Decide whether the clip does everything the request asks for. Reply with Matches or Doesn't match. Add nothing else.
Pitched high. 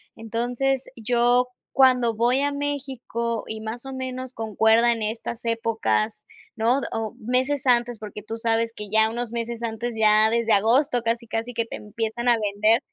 Matches